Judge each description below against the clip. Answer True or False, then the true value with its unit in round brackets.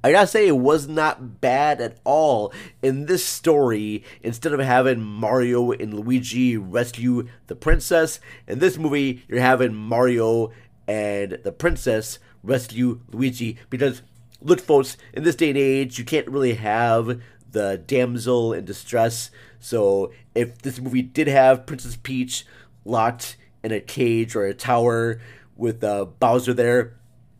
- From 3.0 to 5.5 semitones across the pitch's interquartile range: False (2.4 semitones)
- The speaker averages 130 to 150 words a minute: True (145 wpm)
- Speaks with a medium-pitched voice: False (125 Hz)